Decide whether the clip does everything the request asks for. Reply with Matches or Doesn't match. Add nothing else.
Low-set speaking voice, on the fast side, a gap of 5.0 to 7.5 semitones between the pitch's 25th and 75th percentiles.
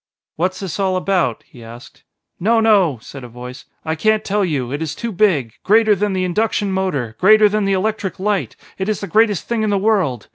Doesn't match